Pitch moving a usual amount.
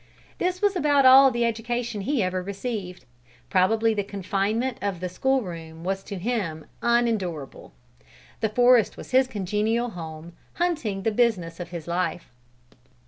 Yes: average, 5.0 semitones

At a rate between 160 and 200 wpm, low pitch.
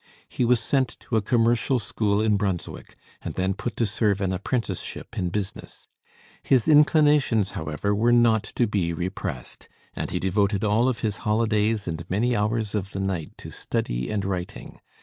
Yes: average, 170 wpm; low, 105 Hz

